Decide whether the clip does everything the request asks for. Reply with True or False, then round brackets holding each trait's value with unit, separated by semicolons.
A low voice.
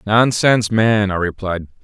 True (105 Hz)